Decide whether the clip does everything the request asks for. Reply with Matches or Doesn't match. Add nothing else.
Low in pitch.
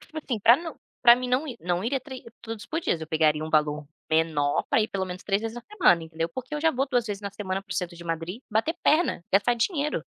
Doesn't match